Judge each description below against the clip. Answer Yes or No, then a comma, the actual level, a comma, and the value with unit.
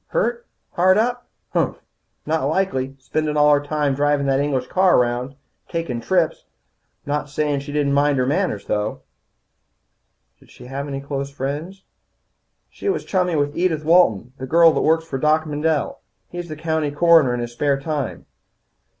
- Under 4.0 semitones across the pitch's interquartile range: Yes, average, 3.2 semitones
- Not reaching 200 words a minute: Yes, average, 165 wpm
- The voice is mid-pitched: Yes, medium, 145 Hz